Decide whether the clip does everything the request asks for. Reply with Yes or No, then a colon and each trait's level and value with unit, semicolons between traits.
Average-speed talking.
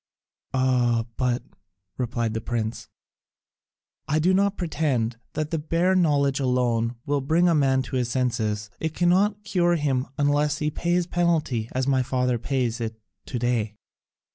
Yes: average, 155 wpm